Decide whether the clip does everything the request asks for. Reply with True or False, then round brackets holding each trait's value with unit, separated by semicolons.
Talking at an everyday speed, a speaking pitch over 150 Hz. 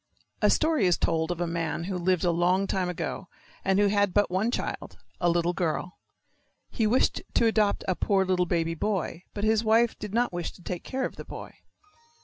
False (210 wpm; 185 Hz)